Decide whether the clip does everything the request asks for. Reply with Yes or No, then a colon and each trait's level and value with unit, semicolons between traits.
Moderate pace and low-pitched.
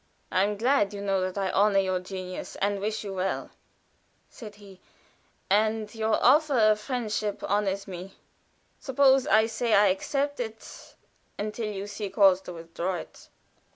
No: average, 155 wpm; high, 205 Hz